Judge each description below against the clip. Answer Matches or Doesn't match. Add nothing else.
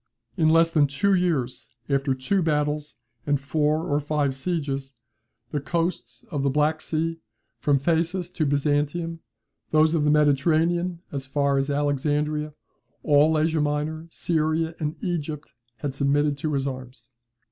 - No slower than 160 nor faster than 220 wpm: Doesn't match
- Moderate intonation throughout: Doesn't match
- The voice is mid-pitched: Matches